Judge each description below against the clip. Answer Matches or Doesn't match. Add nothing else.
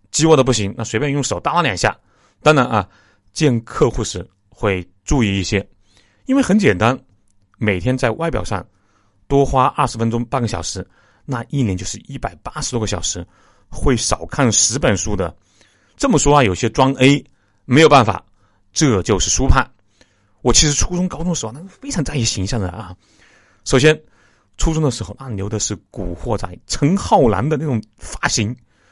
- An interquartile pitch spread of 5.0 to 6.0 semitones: Matches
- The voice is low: Matches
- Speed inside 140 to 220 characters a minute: Doesn't match